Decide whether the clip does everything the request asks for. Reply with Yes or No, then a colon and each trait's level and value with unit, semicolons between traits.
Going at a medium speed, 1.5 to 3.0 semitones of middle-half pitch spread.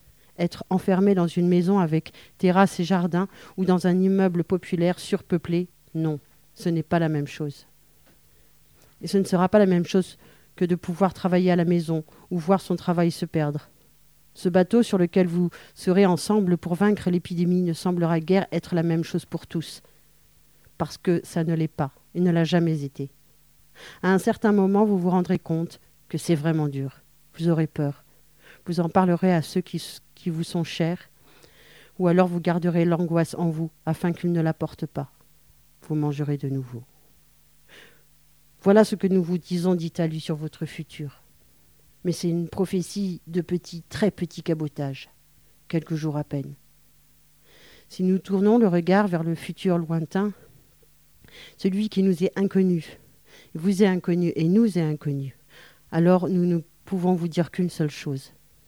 Yes: average, 175 wpm; average, 2.7 semitones